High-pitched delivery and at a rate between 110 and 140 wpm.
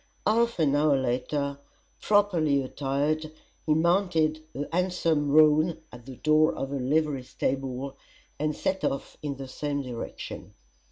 No: medium, 150 Hz; slow, 135 wpm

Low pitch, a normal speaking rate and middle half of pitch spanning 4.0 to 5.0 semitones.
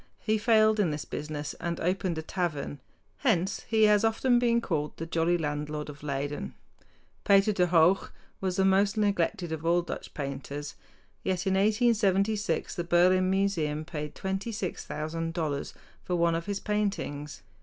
No: medium, 180 Hz; average, 150 wpm; average, 4.7 semitones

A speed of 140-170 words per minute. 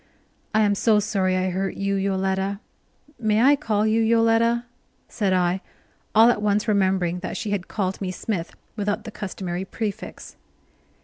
Yes: average, 160 wpm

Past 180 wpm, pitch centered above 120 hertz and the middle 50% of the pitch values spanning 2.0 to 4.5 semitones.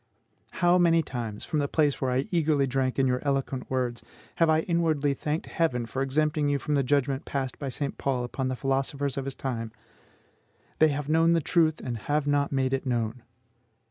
Yes: average, 200 wpm; medium, 140 Hz; average, 2.8 semitones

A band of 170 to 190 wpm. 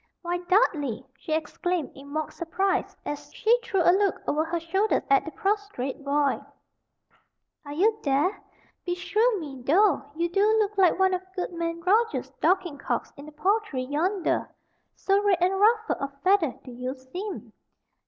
No: average, 160 wpm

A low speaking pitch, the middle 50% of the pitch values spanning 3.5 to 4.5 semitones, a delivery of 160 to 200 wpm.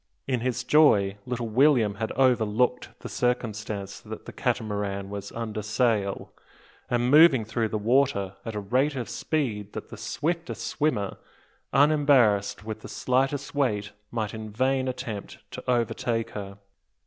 No: low, 115 Hz; average, 3.9 semitones; average, 145 wpm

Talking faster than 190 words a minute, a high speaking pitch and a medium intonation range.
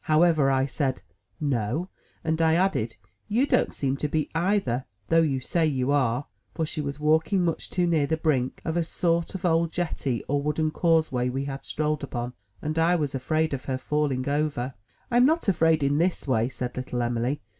No: average, 200 wpm; medium, 150 Hz; average, 3.7 semitones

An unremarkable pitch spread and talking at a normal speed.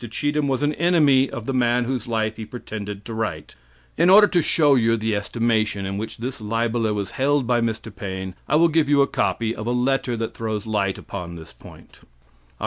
No: average, 4.3 semitones; fast, 215 wpm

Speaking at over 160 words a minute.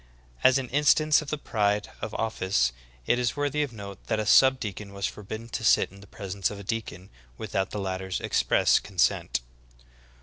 Yes: fast, 205 wpm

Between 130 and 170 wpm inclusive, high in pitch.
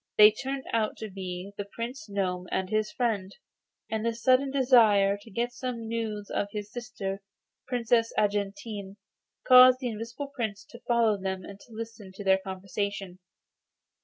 Yes: average, 160 wpm; high, 215 Hz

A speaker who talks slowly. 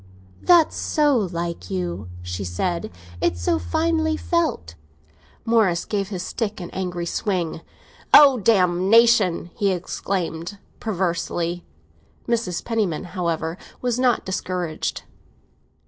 Yes: slow, 105 wpm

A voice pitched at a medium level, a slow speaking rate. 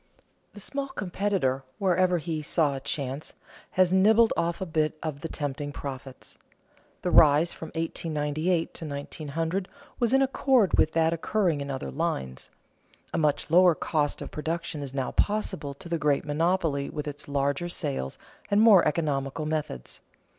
No: medium, 160 Hz; average, 155 wpm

